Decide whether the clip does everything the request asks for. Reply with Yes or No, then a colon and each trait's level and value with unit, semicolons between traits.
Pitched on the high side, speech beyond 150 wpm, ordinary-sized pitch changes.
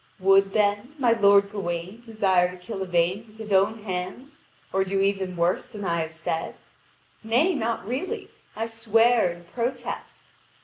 Yes: high, 200 Hz; average, 160 wpm; average, 3.6 semitones